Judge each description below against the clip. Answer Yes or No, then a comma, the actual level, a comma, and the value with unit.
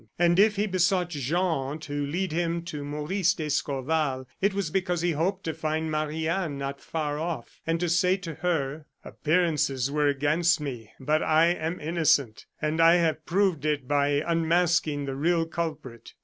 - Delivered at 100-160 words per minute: No, average, 170 wpm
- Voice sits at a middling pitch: Yes, medium, 160 Hz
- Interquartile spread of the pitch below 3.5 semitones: Yes, average, 3.0 semitones